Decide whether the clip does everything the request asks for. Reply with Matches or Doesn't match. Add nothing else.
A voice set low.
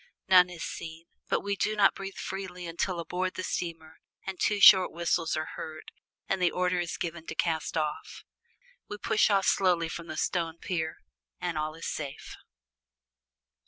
Doesn't match